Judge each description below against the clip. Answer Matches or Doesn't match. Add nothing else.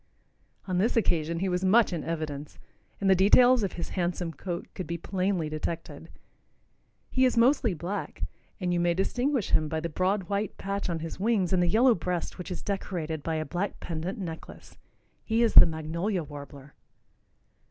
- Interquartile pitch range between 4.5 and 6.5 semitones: Doesn't match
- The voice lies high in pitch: Doesn't match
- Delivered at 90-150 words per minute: Doesn't match